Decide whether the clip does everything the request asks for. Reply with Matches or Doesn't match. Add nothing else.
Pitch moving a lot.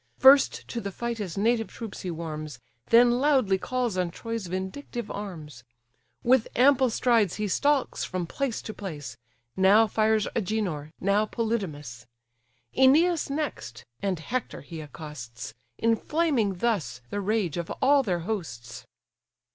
Matches